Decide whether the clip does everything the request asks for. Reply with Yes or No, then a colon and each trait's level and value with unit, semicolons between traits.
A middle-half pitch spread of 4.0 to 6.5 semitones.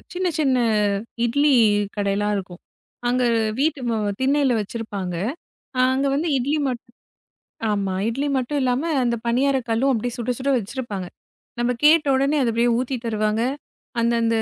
No: average, 3.5 semitones